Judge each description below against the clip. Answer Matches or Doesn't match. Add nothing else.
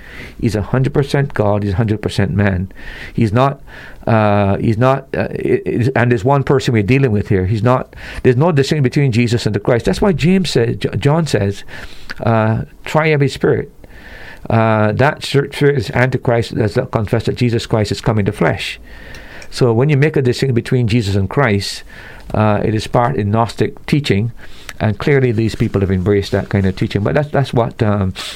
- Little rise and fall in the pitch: Doesn't match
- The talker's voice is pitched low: Matches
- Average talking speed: Matches